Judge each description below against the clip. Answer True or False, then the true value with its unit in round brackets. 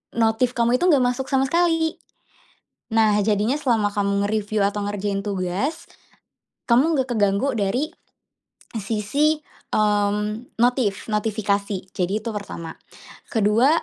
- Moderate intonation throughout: True (3.7 semitones)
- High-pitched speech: True (215 Hz)